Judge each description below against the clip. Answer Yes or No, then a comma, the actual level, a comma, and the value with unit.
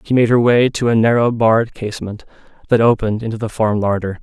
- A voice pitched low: Yes, low, 110 Hz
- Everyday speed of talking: No, fast, 215 wpm